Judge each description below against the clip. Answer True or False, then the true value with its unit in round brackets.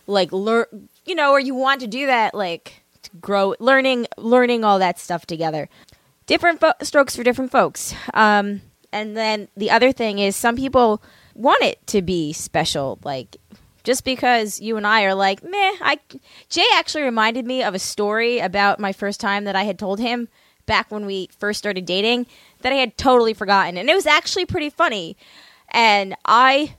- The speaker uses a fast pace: False (190 wpm)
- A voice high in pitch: True (220 Hz)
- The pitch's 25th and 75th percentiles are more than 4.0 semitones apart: True (4.4 semitones)